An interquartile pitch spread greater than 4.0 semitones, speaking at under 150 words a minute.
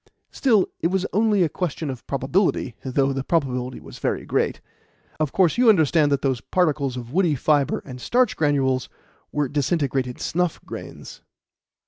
No: average, 5.2 semitones; average, 155 wpm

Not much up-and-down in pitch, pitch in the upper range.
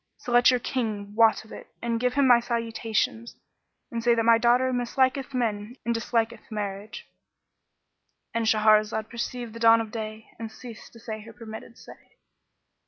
Yes: narrow, 1.6 semitones; high, 230 Hz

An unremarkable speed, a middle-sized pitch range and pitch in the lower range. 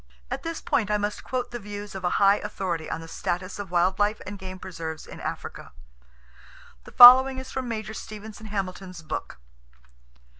No: average, 180 wpm; average, 3.0 semitones; high, 205 Hz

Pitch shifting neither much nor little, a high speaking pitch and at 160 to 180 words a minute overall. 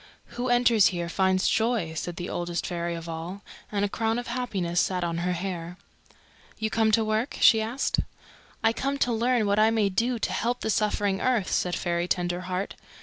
No: average, 4.4 semitones; high, 200 Hz; average, 195 wpm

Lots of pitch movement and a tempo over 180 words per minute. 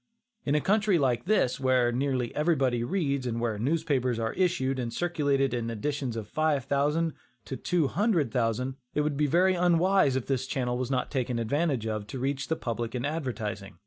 No: average, 4.3 semitones; average, 190 wpm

